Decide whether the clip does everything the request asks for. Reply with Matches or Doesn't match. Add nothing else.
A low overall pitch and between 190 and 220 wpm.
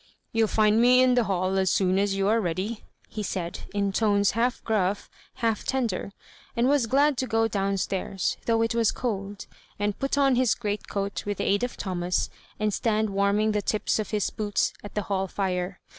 Doesn't match